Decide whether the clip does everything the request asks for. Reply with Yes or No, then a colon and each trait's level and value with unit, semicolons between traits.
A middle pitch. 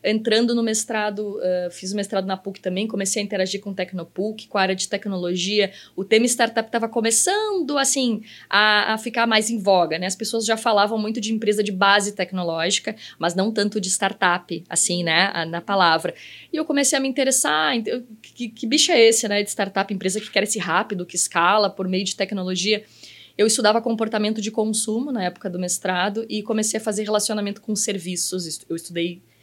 No: high, 210 Hz